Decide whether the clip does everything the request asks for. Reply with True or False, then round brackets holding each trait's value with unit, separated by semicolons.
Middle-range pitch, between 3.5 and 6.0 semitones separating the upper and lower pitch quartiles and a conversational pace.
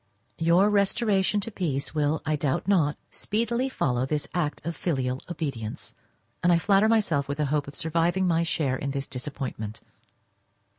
True (160 Hz; 5.4 semitones; 160 wpm)